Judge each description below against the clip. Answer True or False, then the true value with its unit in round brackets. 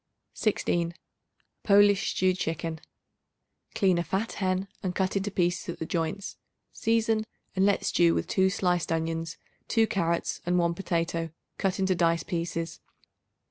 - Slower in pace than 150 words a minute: True (140 wpm)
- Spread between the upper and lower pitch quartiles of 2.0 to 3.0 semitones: True (2.7 semitones)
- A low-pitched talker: False (180 Hz)